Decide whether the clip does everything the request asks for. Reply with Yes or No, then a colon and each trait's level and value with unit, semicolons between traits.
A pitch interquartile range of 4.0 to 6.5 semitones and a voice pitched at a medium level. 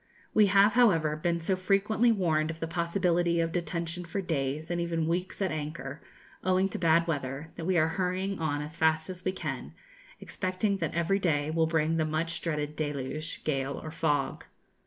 No: average, 2.9 semitones; medium, 165 Hz